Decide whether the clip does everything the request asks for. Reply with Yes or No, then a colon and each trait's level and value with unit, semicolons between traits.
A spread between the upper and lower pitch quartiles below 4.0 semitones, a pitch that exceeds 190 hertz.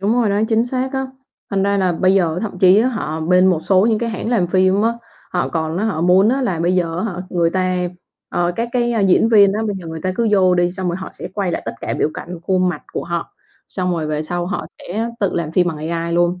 No: average, 3.2 semitones; medium, 185 Hz